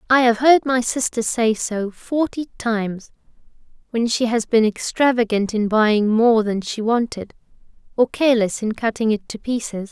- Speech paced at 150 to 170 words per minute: Yes, average, 165 wpm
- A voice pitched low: No, high, 230 Hz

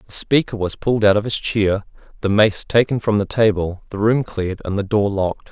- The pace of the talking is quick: Yes, fast, 230 wpm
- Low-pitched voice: Yes, low, 105 Hz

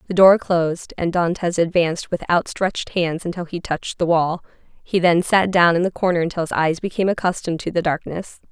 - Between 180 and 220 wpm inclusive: Yes, fast, 205 wpm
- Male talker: No, female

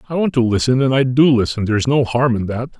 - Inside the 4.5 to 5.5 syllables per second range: No, 6.1 syllables/s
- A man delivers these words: Yes, male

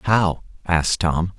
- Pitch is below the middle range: Yes, very low, 90 Hz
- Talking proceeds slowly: Yes, slow, 130 wpm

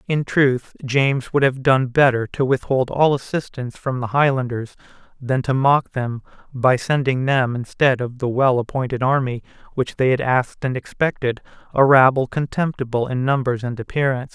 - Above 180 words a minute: No, average, 165 wpm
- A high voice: No, low, 130 Hz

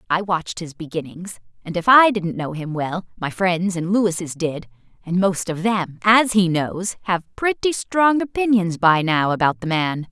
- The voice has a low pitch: No, medium, 185 Hz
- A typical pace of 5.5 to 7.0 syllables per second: No, 4.5 syllables/s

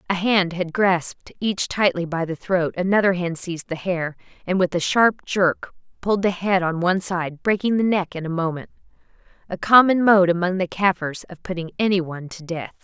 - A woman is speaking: Yes, female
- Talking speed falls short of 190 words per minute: No, average, 195 wpm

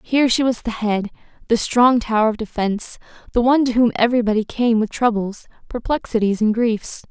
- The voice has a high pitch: Yes, high, 230 Hz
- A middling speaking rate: Yes, average, 175 wpm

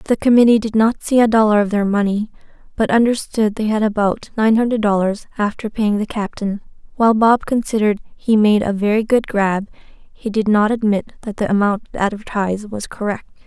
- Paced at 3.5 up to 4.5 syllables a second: No, 5.3 syllables/s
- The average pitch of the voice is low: No, high, 215 Hz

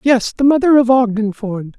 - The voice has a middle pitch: No, high, 235 Hz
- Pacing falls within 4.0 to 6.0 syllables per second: Yes, 4.9 syllables/s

